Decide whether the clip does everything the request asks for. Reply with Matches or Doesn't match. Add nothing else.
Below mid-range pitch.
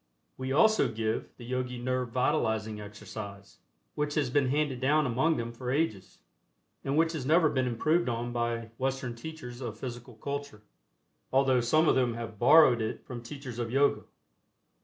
Matches